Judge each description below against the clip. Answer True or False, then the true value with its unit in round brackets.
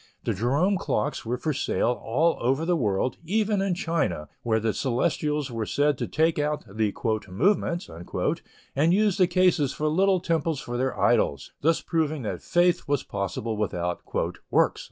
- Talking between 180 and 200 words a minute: False (165 wpm)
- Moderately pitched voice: True (150 Hz)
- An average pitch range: False (6.9 semitones)